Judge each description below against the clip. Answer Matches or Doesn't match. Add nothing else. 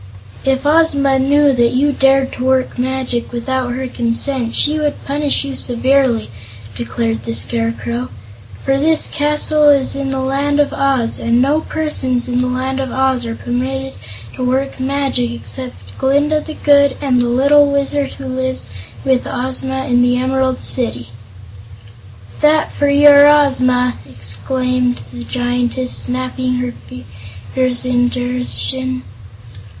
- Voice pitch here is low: Doesn't match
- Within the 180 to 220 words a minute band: Doesn't match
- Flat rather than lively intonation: Matches